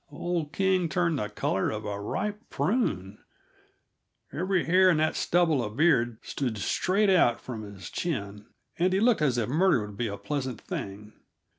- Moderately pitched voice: Yes, medium, 145 Hz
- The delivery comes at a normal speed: Yes, average, 170 wpm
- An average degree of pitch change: No, wide, 9.0 semitones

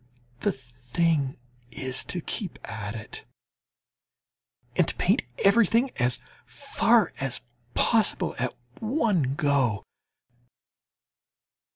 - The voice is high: No, medium, 140 Hz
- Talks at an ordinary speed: No, slow, 90 wpm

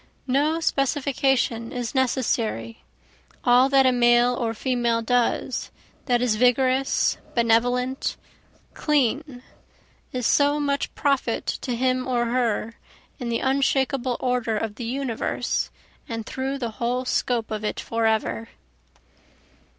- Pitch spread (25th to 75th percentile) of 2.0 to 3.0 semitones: Yes, narrow, 2.4 semitones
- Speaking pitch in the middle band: No, very high, 250 Hz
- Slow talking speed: Yes, slow, 120 wpm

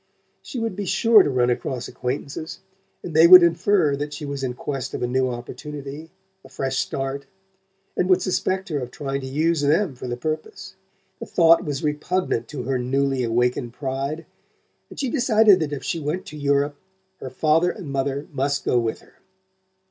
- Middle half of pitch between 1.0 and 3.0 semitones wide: No, average, 4.0 semitones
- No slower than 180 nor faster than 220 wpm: Yes, average, 185 wpm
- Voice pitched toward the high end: No, medium, 145 Hz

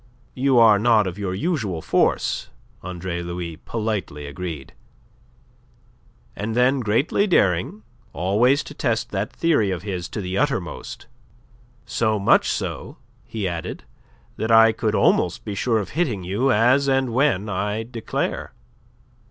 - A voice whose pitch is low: Yes, low, 105 Hz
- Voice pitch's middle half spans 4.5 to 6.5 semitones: Yes, average, 4.8 semitones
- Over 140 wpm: No, slow, 135 wpm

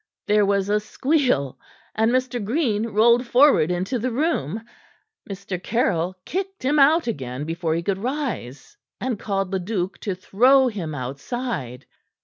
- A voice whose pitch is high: Yes, high, 210 Hz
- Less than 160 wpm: Yes, average, 140 wpm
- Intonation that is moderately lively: No, wide, 6.2 semitones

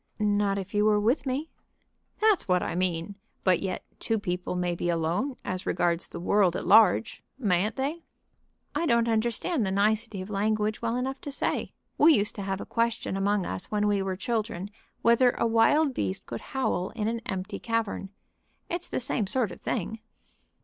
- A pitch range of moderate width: Yes, average, 3.7 semitones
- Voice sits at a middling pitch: No, high, 210 Hz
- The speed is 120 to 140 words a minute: No, average, 185 wpm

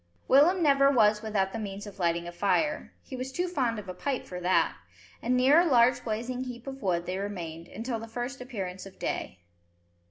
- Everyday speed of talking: No, fast, 210 wpm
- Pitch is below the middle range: No, high, 230 Hz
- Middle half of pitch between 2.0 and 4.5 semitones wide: No, average, 5.3 semitones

